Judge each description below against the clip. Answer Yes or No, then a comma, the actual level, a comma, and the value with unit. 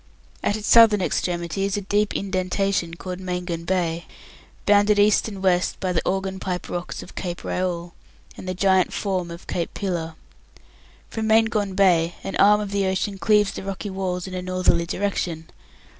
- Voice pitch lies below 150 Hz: No, high, 190 Hz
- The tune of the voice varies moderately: No, narrow, 2.1 semitones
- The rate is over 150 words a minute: Yes, average, 175 wpm